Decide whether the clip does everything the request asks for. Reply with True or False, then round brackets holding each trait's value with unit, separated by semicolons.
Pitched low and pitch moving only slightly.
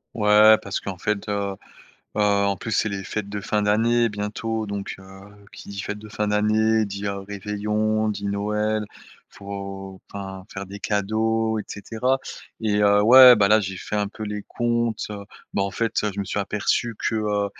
True (105 Hz; 1.4 semitones)